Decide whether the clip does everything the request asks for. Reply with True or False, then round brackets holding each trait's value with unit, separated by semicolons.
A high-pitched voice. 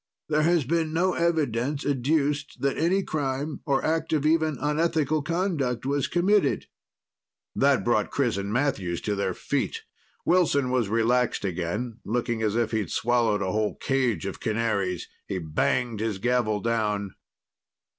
False (125 Hz)